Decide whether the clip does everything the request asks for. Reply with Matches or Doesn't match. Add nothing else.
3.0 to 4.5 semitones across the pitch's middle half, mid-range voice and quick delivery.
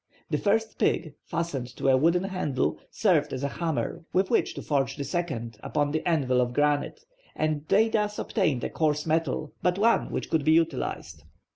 Doesn't match